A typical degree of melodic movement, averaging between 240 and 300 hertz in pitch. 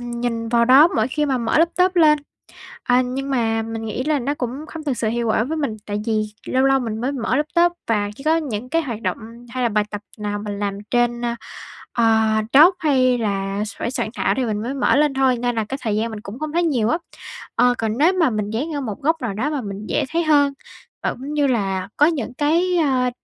Yes: average, 4.9 semitones; very high, 250 Hz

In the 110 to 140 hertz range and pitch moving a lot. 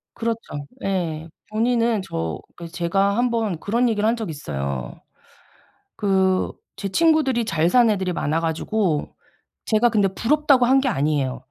No: high, 200 Hz; wide, 6.2 semitones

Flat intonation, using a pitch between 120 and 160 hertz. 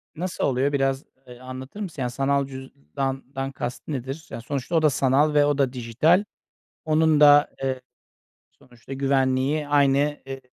Yes: narrow, 2.0 semitones; low, 135 Hz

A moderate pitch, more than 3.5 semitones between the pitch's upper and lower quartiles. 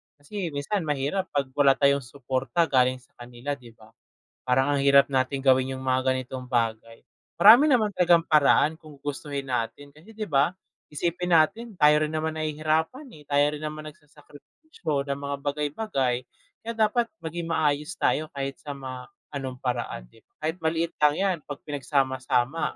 No: medium, 145 Hz; average, 3.2 semitones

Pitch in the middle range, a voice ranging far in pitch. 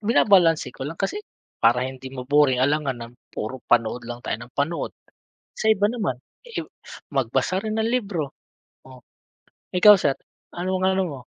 Yes: medium, 145 Hz; wide, 7.1 semitones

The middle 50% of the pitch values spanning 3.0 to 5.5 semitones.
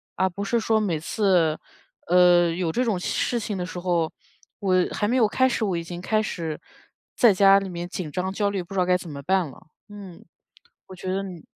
No: narrow, 2.6 semitones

